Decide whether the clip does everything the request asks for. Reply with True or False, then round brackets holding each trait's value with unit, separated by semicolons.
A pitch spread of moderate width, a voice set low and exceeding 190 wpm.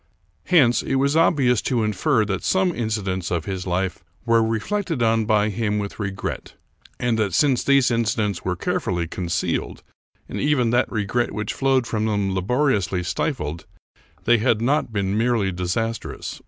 False (4.1 semitones; 110 Hz; 165 wpm)